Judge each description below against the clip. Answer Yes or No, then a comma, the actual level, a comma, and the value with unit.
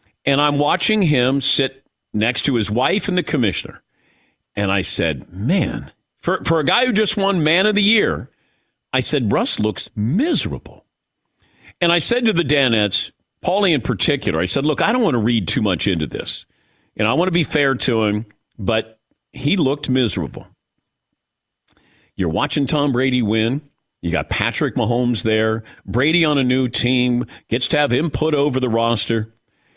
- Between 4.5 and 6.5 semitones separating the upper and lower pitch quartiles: Yes, average, 5.2 semitones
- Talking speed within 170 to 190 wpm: Yes, average, 175 wpm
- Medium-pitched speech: No, low, 125 Hz